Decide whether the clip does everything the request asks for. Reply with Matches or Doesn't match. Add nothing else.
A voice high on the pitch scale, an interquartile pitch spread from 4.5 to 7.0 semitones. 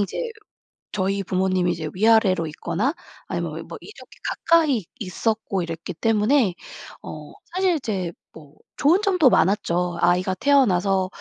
Matches